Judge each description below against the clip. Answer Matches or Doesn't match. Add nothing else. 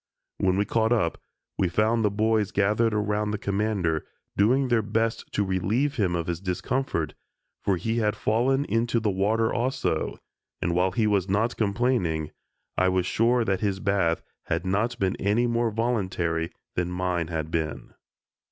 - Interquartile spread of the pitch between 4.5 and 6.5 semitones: Doesn't match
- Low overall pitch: Matches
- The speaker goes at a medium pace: Matches